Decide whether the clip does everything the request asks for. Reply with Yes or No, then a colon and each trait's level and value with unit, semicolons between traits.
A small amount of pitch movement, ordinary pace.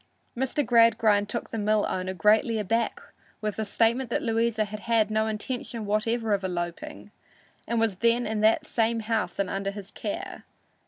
Yes: narrow, 2.0 semitones; average, 170 wpm